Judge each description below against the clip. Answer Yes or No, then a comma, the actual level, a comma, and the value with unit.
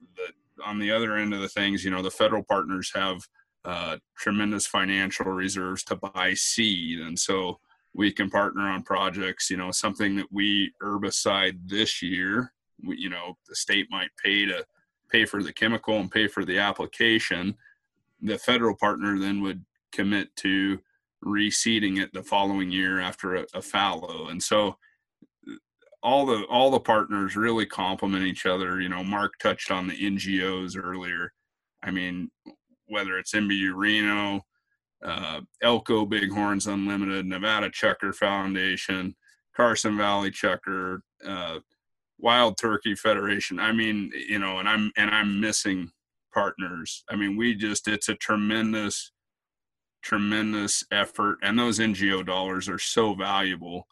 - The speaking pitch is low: Yes, low, 100 Hz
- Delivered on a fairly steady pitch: Yes, narrow, 2.0 semitones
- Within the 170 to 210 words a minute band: No, average, 150 wpm